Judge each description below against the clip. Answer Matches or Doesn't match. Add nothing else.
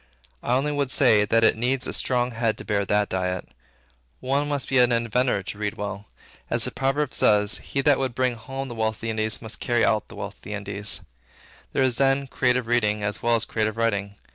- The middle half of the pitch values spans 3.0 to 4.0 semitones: Matches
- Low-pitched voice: Matches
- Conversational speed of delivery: Doesn't match